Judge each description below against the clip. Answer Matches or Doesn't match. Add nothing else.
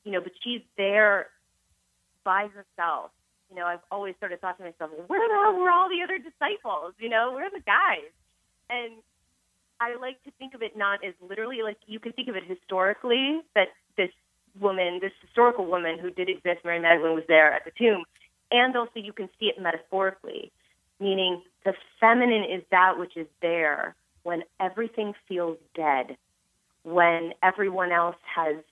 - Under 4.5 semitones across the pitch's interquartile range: Doesn't match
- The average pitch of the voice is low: Doesn't match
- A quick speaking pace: Doesn't match